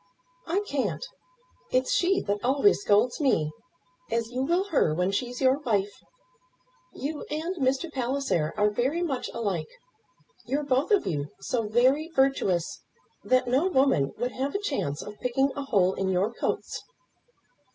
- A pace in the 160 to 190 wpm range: No, average, 150 wpm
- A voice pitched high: Yes, very high, 255 Hz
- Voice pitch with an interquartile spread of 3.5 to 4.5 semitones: No, wide, 5.6 semitones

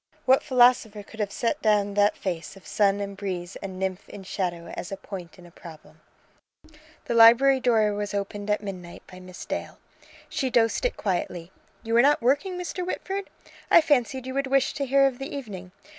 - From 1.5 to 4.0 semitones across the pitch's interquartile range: No, wide, 5.5 semitones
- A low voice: No, high, 210 Hz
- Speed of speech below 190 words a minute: No, average, 195 wpm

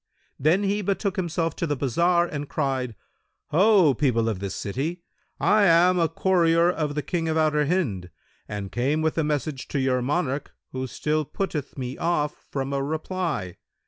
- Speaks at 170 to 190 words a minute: Yes, average, 175 wpm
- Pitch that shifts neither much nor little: Yes, average, 4.5 semitones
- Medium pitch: Yes, medium, 155 Hz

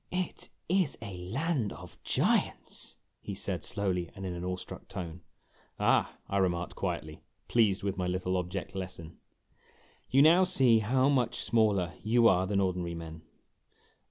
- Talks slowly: No, average, 155 wpm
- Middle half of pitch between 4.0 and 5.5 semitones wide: Yes, average, 4.5 semitones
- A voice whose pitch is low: Yes, very low, 95 Hz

